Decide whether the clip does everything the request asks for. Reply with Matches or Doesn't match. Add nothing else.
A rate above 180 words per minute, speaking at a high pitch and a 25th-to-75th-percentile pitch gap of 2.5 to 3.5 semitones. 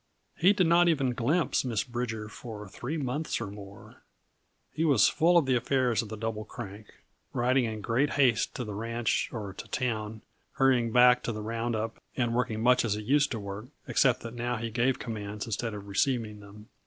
Doesn't match